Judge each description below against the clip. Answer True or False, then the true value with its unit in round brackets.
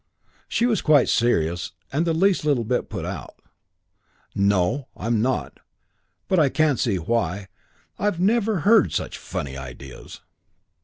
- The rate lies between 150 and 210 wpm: False (140 wpm)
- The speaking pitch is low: True (120 Hz)